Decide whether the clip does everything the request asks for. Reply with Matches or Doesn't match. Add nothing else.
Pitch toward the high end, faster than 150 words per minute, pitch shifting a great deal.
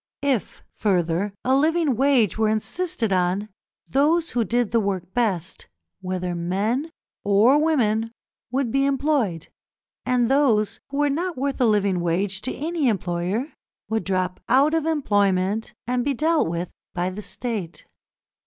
Doesn't match